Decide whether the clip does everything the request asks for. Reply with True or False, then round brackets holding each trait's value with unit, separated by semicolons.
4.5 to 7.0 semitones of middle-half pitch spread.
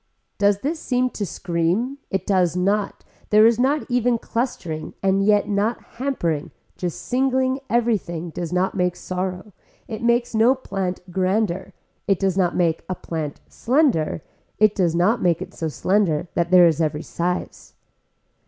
True (5.2 semitones)